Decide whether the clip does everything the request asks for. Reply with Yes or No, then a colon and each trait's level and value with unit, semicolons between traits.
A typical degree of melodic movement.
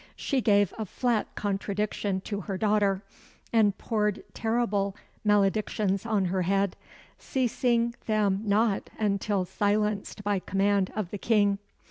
No: narrow, 1.5 semitones